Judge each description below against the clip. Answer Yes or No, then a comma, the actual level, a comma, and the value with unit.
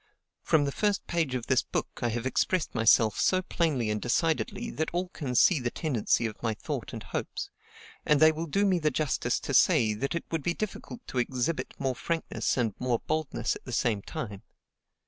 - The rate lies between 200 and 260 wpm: Yes, fast, 205 wpm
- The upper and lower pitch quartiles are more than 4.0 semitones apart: Yes, wide, 5.6 semitones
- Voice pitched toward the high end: No, medium, 140 Hz